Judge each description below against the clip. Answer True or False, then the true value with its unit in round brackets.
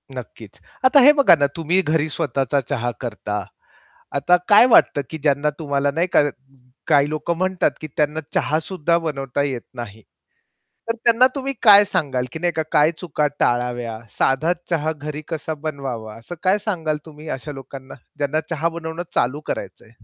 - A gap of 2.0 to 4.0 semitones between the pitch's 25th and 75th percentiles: True (3.7 semitones)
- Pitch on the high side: False (150 Hz)